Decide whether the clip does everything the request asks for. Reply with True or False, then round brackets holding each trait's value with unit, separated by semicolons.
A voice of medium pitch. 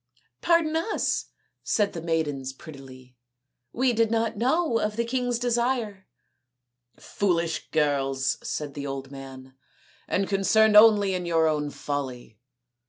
True (165 Hz)